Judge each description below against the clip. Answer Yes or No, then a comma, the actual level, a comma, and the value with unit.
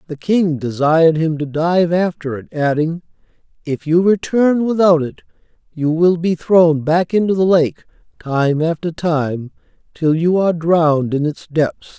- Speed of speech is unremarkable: Yes, average, 160 wpm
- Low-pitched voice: No, medium, 165 Hz